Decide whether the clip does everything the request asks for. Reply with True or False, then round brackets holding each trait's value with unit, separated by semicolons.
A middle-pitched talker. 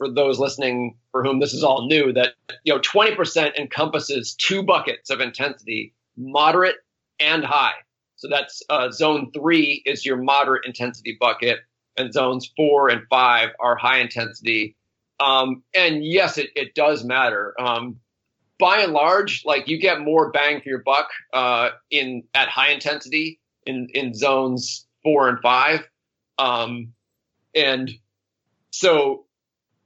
False (130 Hz)